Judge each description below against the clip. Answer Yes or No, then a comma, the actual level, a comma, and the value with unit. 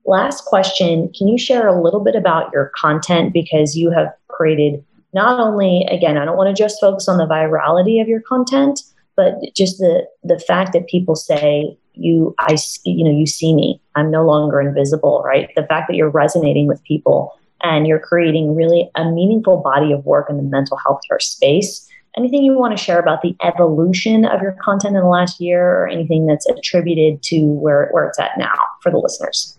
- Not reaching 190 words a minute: No, fast, 205 wpm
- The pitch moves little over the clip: No, average, 4.1 semitones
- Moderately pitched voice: Yes, medium, 170 Hz